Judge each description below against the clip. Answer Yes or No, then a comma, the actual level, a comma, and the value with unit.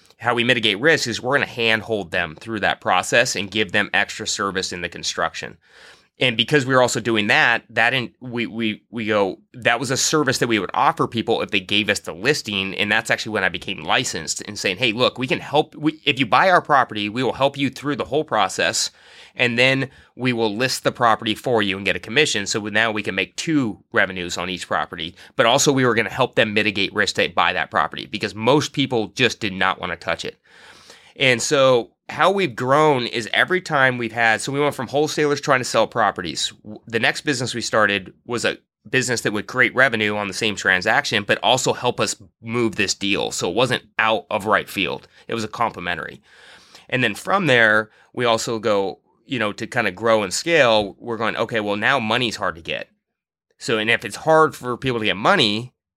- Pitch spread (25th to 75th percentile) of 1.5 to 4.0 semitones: Yes, average, 3.7 semitones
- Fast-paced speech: Yes, fast, 225 wpm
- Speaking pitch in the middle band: No, low, 115 Hz